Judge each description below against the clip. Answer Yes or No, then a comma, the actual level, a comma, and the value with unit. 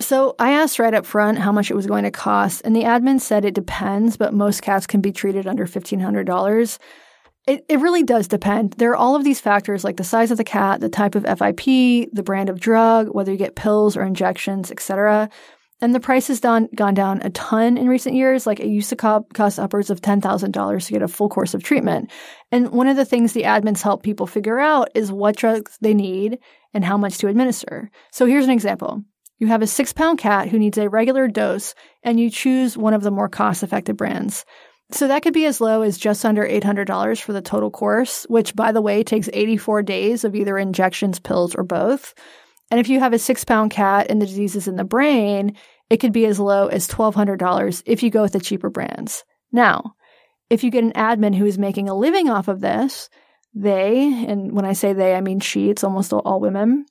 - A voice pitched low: No, high, 215 Hz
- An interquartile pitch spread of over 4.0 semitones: No, average, 3.3 semitones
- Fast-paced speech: Yes, fast, 225 wpm